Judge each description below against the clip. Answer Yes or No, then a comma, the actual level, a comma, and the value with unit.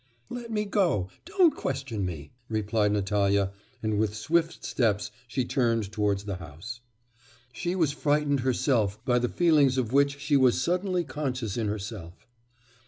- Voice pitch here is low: Yes, low, 120 Hz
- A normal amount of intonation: No, wide, 6.1 semitones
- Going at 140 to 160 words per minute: Yes, average, 150 wpm